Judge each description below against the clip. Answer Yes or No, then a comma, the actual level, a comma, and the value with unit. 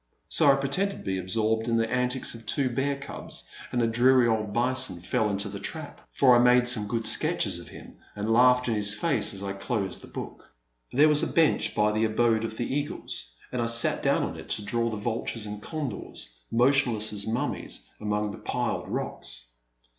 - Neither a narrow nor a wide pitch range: Yes, average, 3.2 semitones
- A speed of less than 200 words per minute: No, fast, 205 wpm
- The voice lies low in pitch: Yes, low, 115 Hz